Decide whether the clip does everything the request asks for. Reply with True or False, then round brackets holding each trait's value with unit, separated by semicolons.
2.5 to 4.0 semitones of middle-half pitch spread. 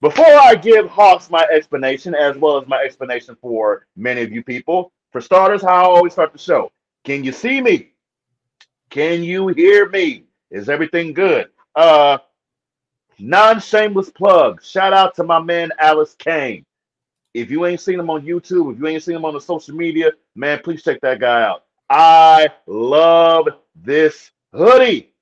False (5.1 semitones)